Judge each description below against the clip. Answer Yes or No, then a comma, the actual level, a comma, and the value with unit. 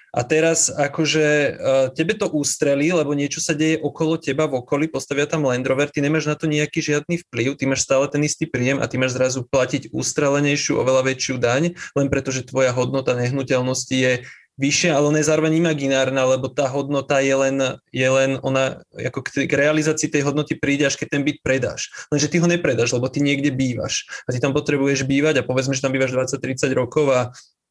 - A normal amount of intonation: No, narrow, 2.3 semitones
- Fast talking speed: Yes, fast, 200 wpm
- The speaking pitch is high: No, medium, 140 Hz